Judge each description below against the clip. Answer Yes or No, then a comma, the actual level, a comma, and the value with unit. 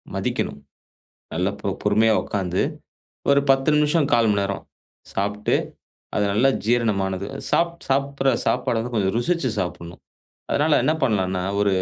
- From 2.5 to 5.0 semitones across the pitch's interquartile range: No, wide, 5.6 semitones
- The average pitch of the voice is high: No, low, 110 Hz